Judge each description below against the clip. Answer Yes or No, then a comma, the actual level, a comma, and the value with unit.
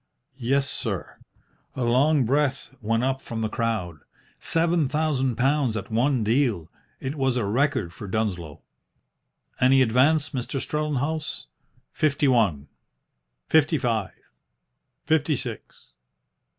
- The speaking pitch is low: Yes, low, 130 Hz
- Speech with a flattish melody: No, average, 4.5 semitones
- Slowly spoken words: Yes, slow, 115 wpm